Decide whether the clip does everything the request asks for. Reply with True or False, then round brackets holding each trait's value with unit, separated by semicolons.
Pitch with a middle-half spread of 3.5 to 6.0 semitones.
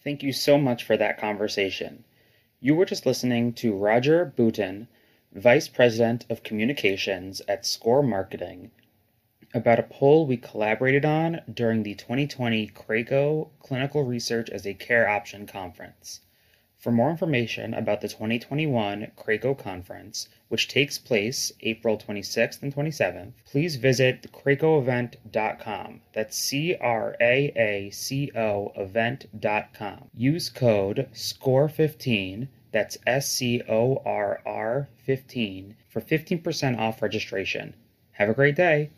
True (4.2 semitones)